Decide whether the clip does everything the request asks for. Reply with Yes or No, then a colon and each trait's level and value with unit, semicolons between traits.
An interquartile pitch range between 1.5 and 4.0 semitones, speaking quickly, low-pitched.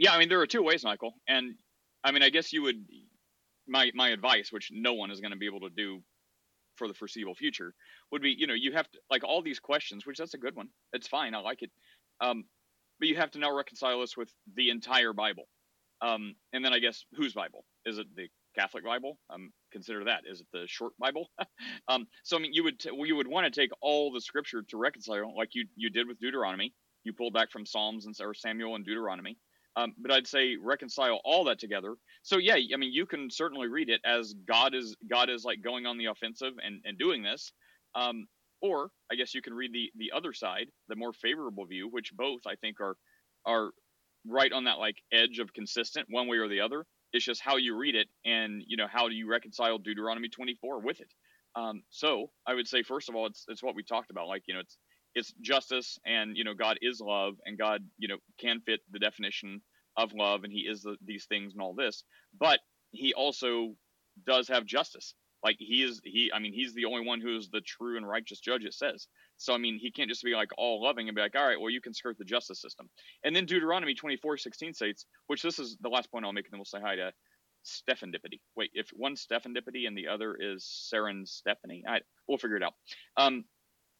Yes: average, 3.3 semitones; fast, 235 wpm; low, 120 Hz